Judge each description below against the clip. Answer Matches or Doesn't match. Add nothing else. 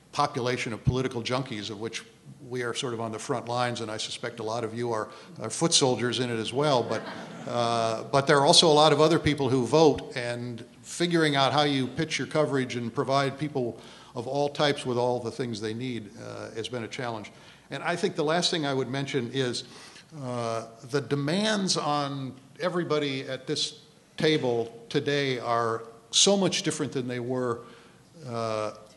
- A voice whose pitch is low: Matches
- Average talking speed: Matches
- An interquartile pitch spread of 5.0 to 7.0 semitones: Doesn't match